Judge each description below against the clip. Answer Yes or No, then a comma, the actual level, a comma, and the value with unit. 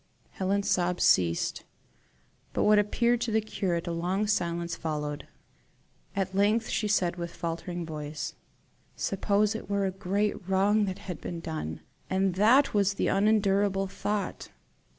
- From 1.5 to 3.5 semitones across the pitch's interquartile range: Yes, average, 3.2 semitones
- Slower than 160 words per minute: Yes, average, 145 wpm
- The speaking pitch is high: Yes, high, 195 Hz